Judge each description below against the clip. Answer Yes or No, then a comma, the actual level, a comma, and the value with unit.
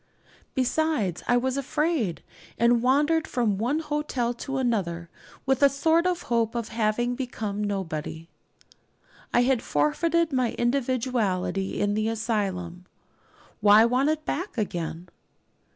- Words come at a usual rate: No, slow, 125 wpm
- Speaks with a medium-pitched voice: No, high, 240 Hz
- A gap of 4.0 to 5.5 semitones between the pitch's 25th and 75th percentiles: Yes, average, 5.0 semitones